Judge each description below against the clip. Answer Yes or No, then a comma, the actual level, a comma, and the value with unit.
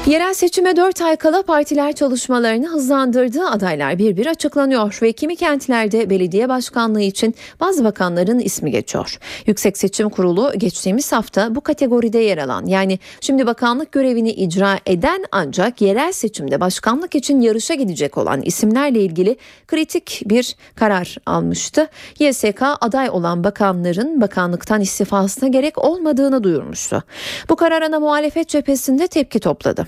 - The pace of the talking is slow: No, average, 135 wpm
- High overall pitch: Yes, high, 240 Hz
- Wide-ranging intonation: Yes, wide, 6.6 semitones